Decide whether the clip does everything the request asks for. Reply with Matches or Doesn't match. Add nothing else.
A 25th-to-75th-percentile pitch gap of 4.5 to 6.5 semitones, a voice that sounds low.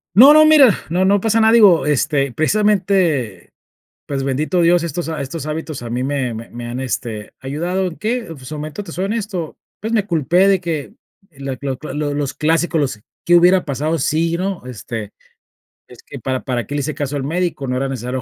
Doesn't match